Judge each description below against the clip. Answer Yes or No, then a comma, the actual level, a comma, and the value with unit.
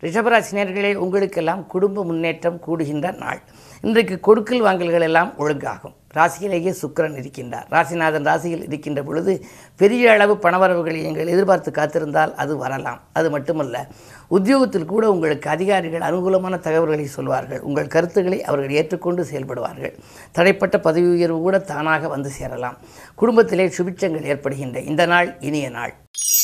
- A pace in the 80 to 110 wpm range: No, average, 120 wpm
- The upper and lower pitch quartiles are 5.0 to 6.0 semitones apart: No, average, 4.2 semitones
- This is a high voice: No, medium, 170 Hz